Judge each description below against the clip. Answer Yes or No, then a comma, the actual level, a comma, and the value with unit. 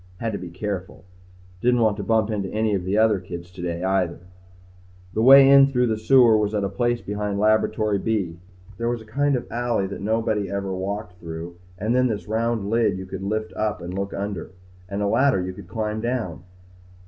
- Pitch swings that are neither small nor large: Yes, average, 3.0 semitones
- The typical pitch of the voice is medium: No, low, 105 Hz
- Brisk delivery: Yes, fast, 215 wpm